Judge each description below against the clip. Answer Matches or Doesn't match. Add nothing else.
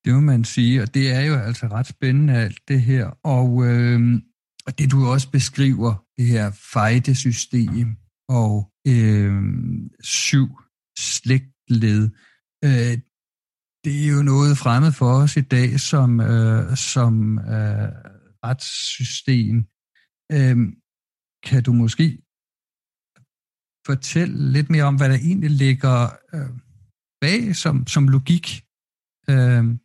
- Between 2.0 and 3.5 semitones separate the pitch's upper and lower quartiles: Matches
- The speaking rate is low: Matches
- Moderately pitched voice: Doesn't match